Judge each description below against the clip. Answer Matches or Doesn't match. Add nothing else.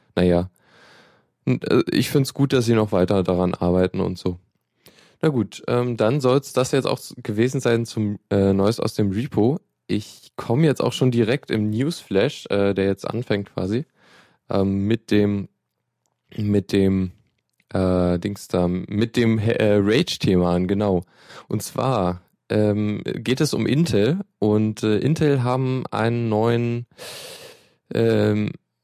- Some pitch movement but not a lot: Matches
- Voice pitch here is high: Doesn't match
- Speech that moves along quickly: Doesn't match